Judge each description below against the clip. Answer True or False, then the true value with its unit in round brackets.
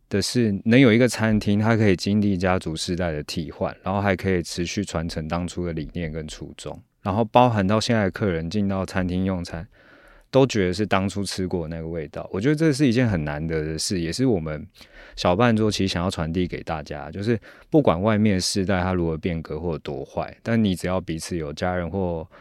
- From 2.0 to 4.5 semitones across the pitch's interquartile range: True (3.9 semitones)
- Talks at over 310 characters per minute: True (320 characters per minute)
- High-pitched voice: False (95 Hz)